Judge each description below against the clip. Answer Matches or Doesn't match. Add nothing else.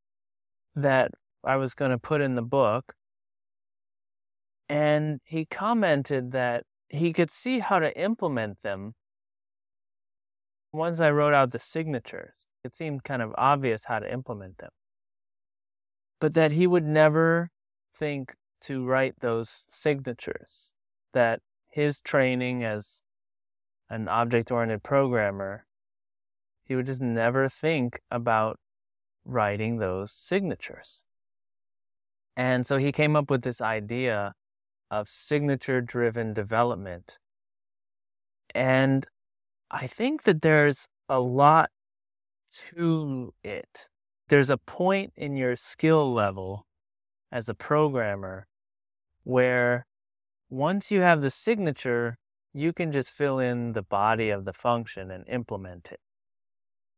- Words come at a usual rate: Doesn't match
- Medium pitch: Doesn't match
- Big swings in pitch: Matches